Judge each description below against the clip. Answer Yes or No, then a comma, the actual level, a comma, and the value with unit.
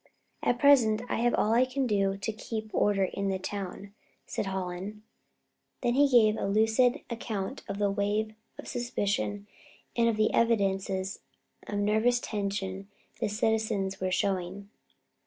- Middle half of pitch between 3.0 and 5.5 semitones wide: No, narrow, 2.6 semitones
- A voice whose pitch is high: Yes, high, 210 Hz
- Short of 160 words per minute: Yes, average, 150 wpm